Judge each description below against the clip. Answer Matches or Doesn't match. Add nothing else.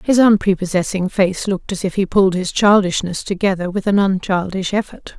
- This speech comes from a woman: Matches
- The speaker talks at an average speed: Matches